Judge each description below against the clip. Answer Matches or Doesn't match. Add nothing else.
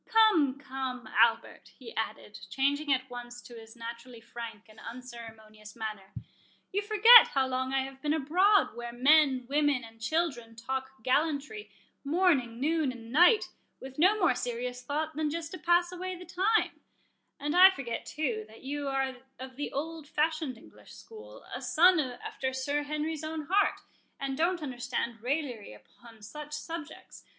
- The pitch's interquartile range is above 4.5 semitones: Matches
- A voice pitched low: Doesn't match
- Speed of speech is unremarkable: Matches